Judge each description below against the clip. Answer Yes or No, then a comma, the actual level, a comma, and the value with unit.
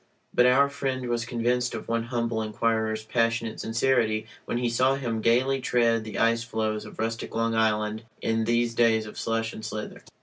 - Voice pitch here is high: No, low, 115 Hz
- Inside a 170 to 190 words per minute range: Yes, average, 180 wpm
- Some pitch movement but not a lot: No, narrow, 1.5 semitones